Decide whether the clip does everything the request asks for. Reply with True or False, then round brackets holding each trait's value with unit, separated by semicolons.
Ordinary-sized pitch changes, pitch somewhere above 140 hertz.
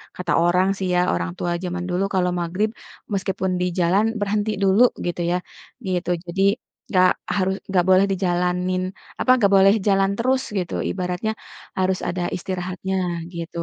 False (1.5 semitones; 185 Hz)